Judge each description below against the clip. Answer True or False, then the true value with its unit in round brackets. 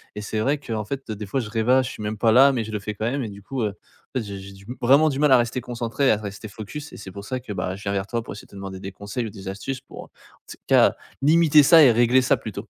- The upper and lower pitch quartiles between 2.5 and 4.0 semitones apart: False (4.4 semitones)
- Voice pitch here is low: True (115 Hz)